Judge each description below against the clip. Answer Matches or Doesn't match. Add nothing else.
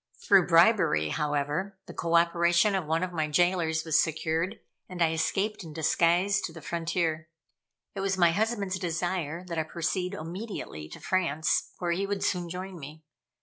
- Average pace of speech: Matches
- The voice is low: Doesn't match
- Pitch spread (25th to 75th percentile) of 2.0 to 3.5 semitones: Matches